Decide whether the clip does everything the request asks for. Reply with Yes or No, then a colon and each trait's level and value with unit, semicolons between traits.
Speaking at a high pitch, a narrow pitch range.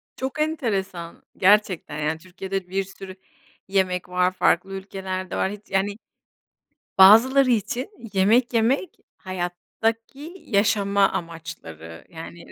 No: high, 195 Hz; average, 3.6 semitones